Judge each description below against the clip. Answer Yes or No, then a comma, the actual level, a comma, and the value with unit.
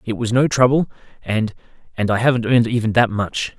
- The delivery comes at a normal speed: Yes, average, 185 wpm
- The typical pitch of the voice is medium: No, low, 115 Hz